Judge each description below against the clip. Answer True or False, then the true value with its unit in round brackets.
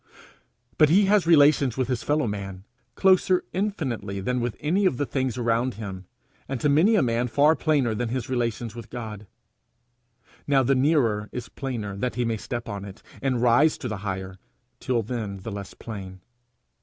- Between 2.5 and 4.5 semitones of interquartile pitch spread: False (5.0 semitones)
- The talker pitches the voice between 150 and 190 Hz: False (120 Hz)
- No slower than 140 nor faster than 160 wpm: False (180 wpm)